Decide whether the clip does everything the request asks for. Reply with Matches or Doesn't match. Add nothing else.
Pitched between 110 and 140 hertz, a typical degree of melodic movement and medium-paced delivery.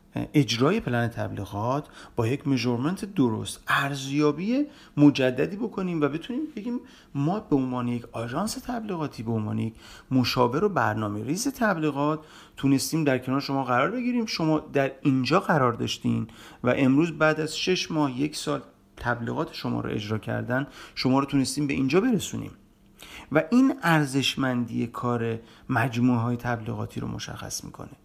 Matches